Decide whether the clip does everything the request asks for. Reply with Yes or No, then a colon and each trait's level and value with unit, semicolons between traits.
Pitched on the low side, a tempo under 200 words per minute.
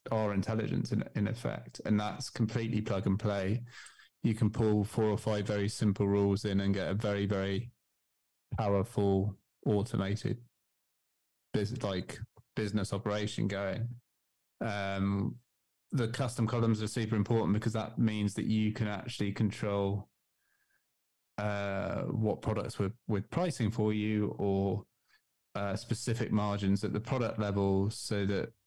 Yes: low, 105 Hz; average, 140 wpm